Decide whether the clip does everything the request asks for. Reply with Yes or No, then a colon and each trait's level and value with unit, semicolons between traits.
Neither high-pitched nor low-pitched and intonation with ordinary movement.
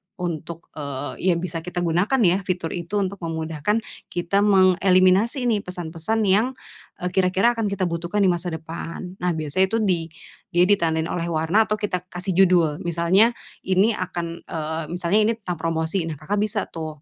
Yes: medium, 180 Hz; average, 3.1 semitones